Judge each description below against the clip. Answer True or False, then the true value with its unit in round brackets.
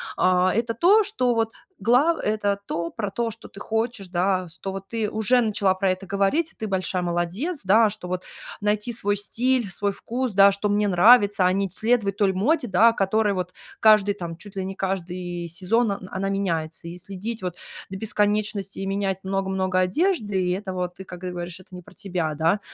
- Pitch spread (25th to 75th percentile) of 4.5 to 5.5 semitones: False (3.0 semitones)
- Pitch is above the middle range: True (195 Hz)